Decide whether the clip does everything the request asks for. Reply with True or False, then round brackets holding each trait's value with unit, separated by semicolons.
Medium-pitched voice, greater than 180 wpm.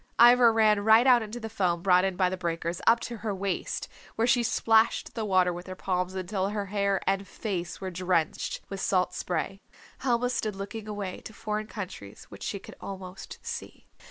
False (195 Hz; 195 wpm)